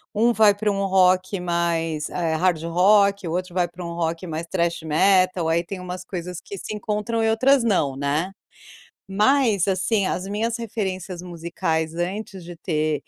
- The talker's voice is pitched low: No, medium, 185 Hz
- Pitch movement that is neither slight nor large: Yes, average, 3.2 semitones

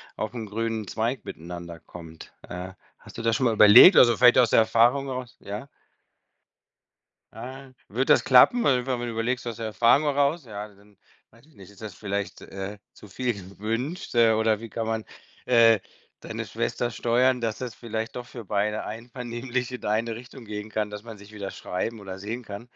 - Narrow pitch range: No, average, 3.0 semitones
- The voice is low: Yes, low, 115 Hz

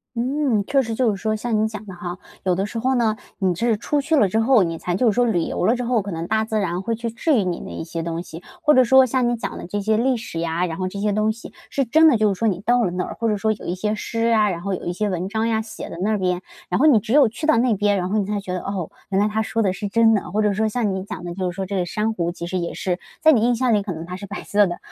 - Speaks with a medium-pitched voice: No, high, 210 Hz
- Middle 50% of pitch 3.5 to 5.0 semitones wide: Yes, average, 3.8 semitones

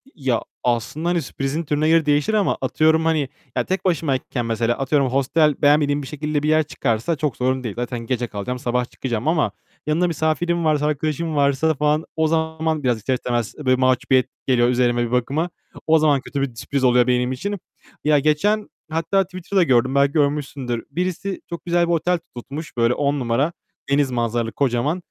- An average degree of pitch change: Yes, average, 4.2 semitones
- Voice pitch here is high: No, medium, 145 Hz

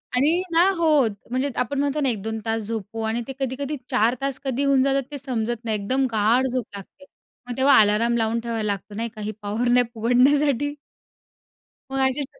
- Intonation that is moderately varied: Yes, average, 3.6 semitones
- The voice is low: No, high, 245 Hz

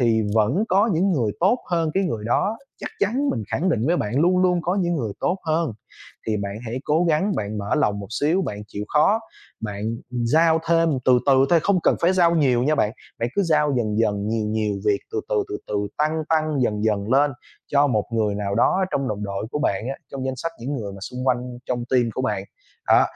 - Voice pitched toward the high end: No, low, 130 Hz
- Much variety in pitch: Yes, wide, 7.7 semitones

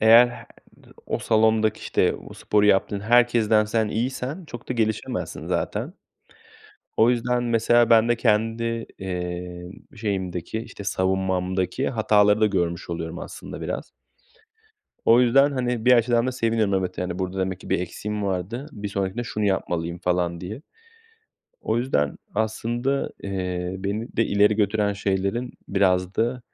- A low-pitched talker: Yes, low, 105 Hz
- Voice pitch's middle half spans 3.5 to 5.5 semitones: Yes, average, 3.9 semitones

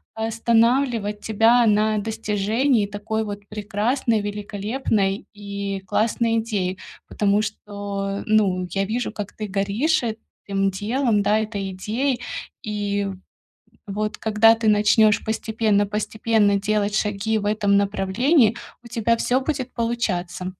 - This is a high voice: Yes, high, 210 Hz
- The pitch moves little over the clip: Yes, narrow, 1.9 semitones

